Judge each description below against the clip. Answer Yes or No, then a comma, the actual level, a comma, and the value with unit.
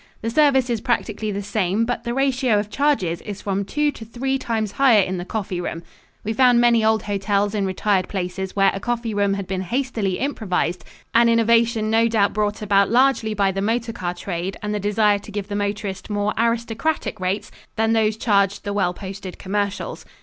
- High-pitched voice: Yes, high, 210 Hz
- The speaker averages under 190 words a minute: No, average, 200 wpm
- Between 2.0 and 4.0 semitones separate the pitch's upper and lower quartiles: Yes, average, 2.8 semitones